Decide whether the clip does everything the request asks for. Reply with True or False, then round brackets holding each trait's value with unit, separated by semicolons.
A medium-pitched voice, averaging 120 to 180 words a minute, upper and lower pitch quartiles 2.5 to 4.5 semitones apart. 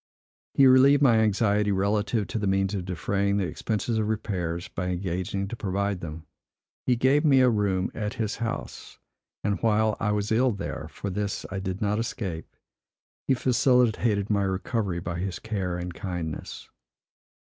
False (100 Hz; 165 wpm; 3.1 semitones)